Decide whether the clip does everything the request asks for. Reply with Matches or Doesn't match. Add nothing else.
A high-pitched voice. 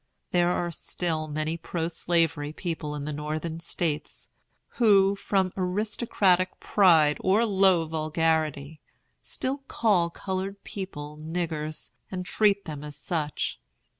Doesn't match